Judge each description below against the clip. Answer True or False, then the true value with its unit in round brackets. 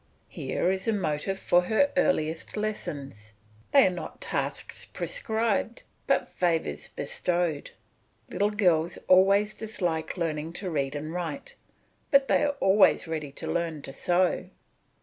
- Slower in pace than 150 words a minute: True (135 wpm)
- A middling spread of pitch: True (5.0 semitones)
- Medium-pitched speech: True (180 Hz)